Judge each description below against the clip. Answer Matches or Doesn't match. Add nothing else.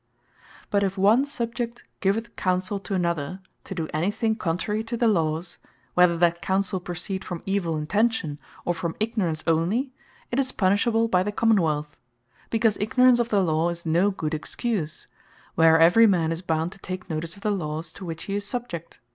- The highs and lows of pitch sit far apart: Doesn't match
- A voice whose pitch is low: Doesn't match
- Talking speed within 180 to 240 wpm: Matches